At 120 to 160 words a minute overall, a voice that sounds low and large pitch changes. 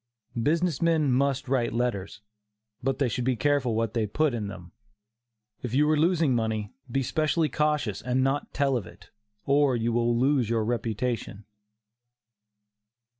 No: average, 155 wpm; low, 125 Hz; average, 4.1 semitones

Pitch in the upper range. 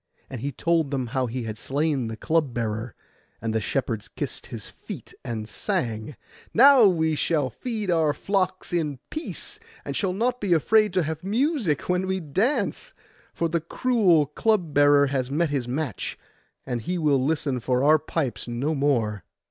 No: medium, 150 Hz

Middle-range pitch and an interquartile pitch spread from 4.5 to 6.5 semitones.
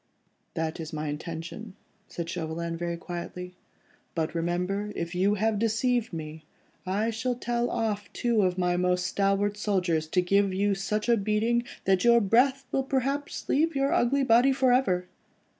No: high, 200 Hz; average, 5.1 semitones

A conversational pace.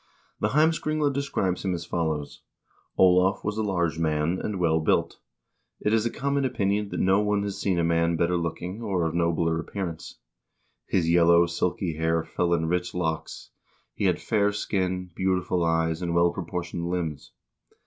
Yes: average, 170 wpm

